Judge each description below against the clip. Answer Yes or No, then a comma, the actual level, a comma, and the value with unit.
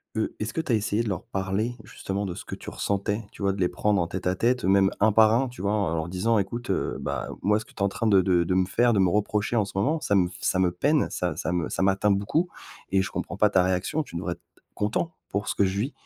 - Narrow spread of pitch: No, average, 3.0 semitones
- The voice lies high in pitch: No, low, 100 Hz